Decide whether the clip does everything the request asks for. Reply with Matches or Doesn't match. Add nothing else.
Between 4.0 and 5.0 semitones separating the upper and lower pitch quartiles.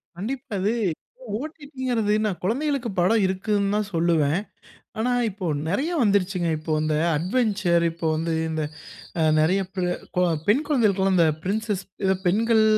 Matches